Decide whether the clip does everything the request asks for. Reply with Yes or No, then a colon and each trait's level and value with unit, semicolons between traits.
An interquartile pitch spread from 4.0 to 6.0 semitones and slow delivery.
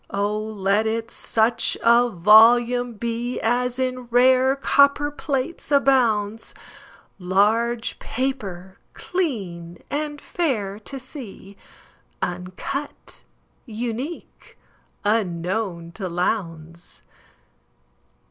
Yes: average, 4.5 semitones; slow, 70 wpm